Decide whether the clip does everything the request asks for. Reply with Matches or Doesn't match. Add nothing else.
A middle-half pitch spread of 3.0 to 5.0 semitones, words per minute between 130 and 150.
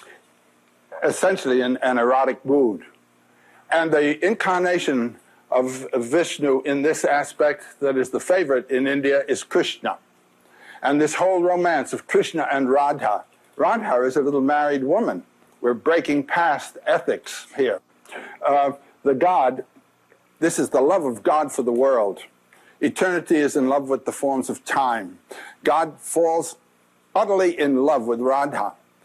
Matches